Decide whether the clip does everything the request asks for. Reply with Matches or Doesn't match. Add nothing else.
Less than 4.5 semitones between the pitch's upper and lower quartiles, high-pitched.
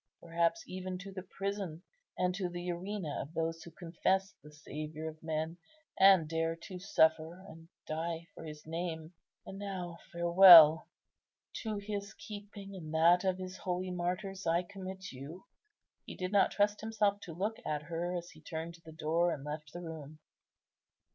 Doesn't match